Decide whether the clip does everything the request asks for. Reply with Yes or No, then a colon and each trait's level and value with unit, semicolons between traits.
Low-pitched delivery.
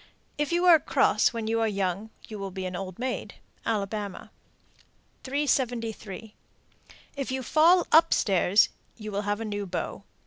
No: high, 220 Hz